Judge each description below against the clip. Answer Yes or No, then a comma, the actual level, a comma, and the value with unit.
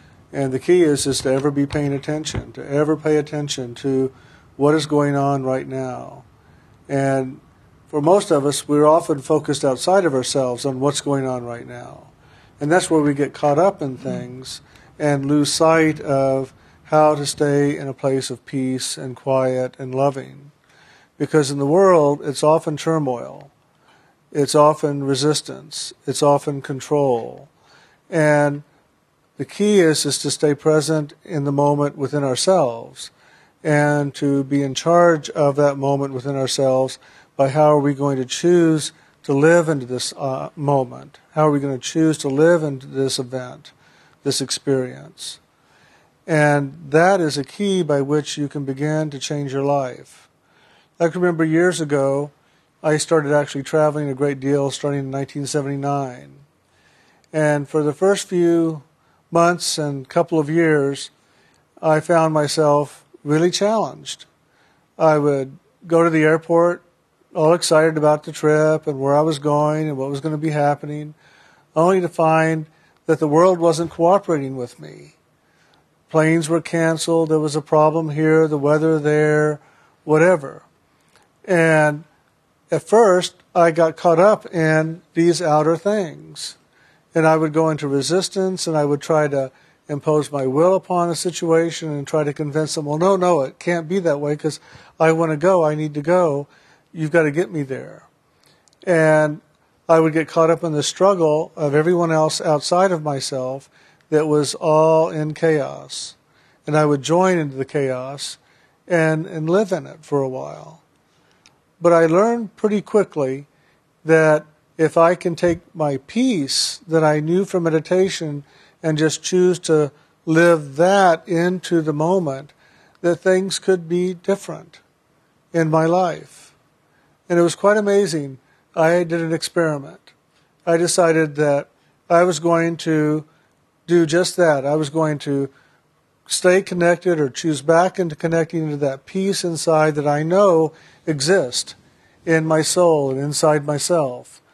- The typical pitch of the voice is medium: Yes, medium, 155 Hz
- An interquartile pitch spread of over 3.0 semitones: No, narrow, 2.6 semitones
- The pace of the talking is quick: No, average, 160 wpm